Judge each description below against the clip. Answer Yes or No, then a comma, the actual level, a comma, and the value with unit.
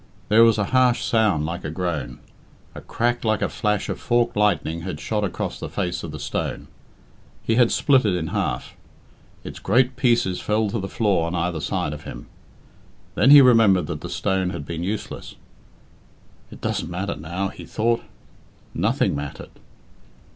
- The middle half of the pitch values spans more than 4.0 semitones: Yes, average, 5.1 semitones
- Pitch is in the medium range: No, low, 100 Hz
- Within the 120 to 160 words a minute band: No, average, 175 wpm